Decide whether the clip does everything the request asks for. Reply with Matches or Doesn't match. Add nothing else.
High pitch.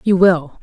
Doesn't match